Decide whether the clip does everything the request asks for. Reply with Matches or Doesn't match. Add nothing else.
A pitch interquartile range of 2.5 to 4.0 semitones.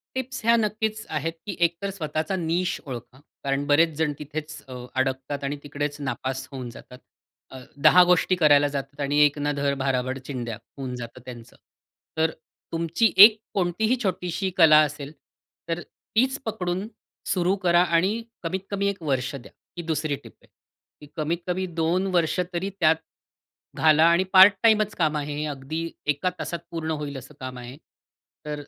Doesn't match